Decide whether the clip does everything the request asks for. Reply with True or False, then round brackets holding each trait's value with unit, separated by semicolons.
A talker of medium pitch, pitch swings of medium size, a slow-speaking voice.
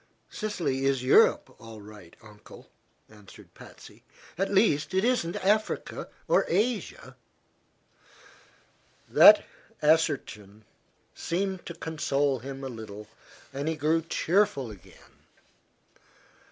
False (145 Hz; 8.9 semitones; 100 wpm)